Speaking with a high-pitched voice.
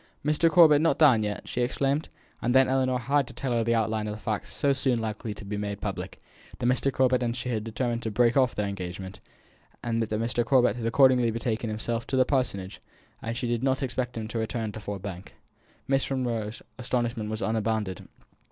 No: low, 115 Hz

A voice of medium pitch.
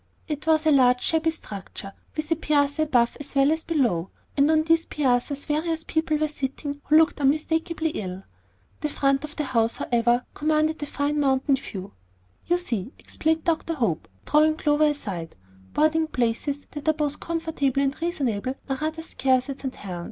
No: very high, 290 Hz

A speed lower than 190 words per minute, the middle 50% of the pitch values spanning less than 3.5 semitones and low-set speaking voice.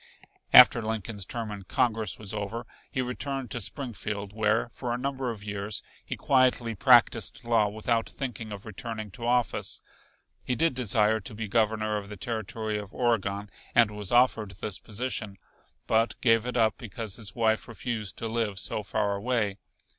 Yes: average, 170 wpm; narrow, 2.4 semitones; low, 110 Hz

